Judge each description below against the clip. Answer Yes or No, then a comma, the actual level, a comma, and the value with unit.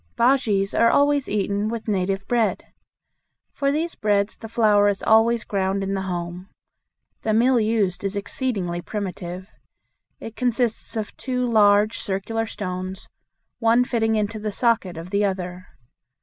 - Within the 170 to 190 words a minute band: No, average, 145 wpm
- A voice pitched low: No, high, 210 Hz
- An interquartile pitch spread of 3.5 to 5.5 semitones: No, average, 3.1 semitones